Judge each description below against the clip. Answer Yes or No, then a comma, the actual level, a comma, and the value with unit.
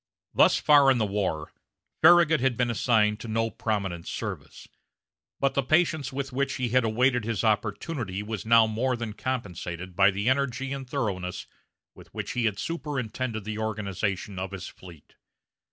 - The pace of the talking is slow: No, average, 160 wpm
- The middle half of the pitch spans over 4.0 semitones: Yes, average, 4.5 semitones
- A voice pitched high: No, low, 115 Hz